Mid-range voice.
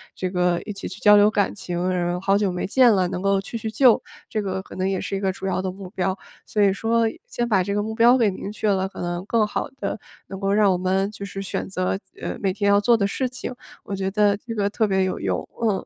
No: high, 195 Hz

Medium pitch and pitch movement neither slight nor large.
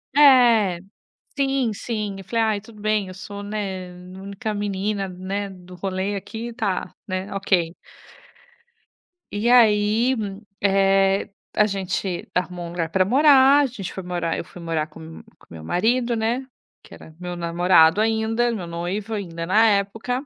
No: high, 200 Hz; average, 3.6 semitones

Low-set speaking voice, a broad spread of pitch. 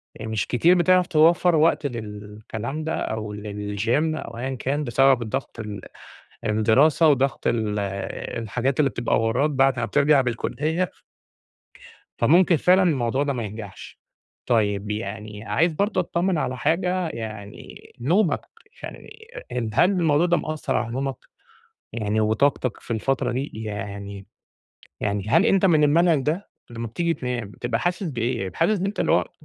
Yes: low, 130 Hz; wide, 6.6 semitones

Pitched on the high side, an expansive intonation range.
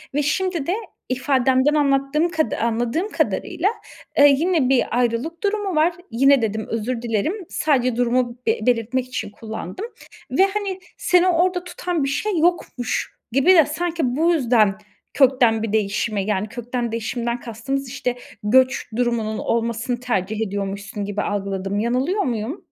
Yes: very high, 250 Hz; wide, 5.7 semitones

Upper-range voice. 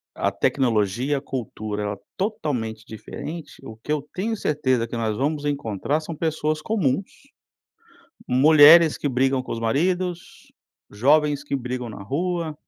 No: medium, 140 Hz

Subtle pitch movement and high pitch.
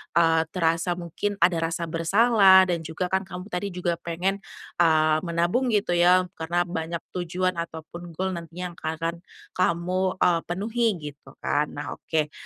No: narrow, 1.9 semitones; medium, 175 Hz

